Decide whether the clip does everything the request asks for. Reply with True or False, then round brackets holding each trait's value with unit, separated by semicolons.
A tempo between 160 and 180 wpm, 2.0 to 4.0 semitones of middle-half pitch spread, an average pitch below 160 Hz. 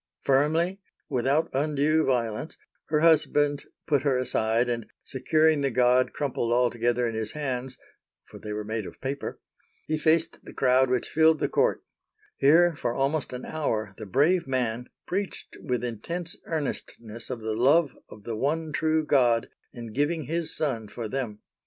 False (165 wpm; 4.6 semitones; 135 Hz)